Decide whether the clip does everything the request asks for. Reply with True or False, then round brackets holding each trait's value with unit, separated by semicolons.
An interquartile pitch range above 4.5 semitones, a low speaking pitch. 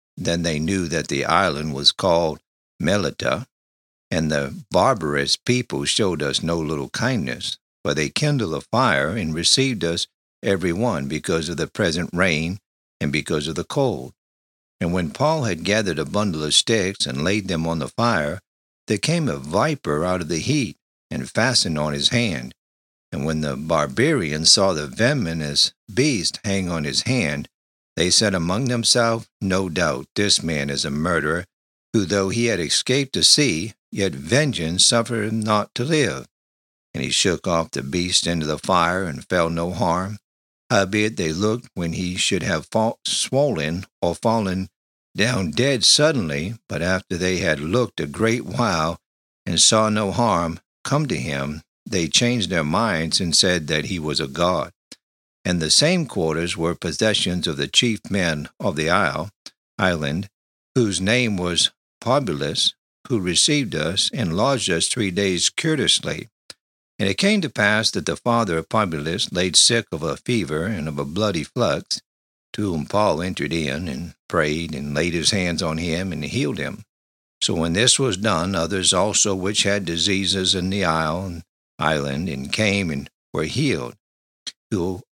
True (5.2 semitones; 90 Hz)